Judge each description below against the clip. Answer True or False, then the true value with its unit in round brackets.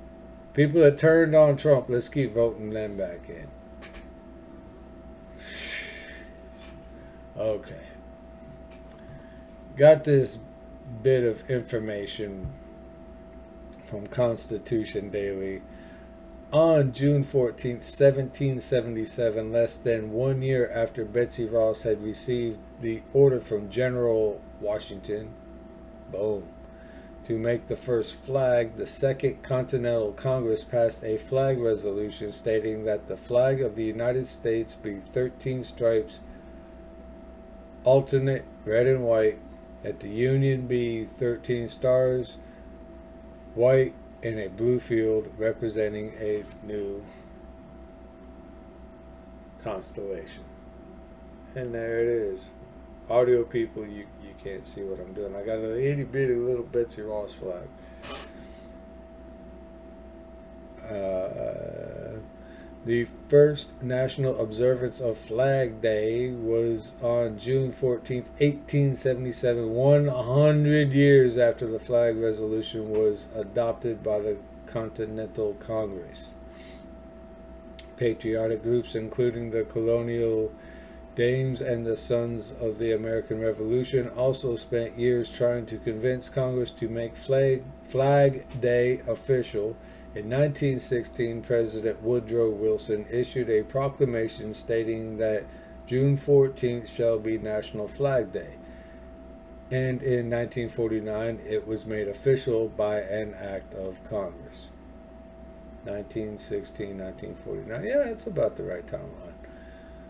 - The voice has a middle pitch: False (115 Hz)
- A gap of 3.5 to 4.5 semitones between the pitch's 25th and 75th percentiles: True (3.9 semitones)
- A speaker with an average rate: False (105 wpm)